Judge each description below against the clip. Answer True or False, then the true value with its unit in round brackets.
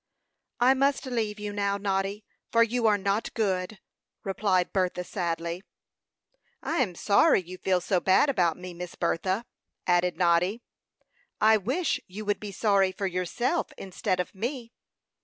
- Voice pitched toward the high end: True (200 Hz)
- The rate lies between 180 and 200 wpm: False (150 wpm)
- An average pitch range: True (3.4 semitones)